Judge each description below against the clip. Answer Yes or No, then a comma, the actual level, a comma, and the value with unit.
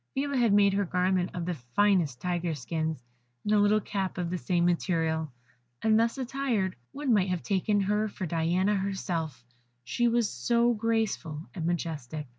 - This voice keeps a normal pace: Yes, average, 170 wpm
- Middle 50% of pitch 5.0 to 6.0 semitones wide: No, average, 4.3 semitones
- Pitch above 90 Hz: Yes, high, 190 Hz